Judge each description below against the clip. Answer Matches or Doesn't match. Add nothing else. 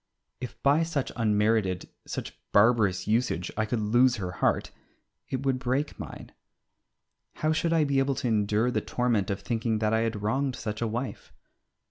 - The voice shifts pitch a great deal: Doesn't match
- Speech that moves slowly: Doesn't match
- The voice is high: Doesn't match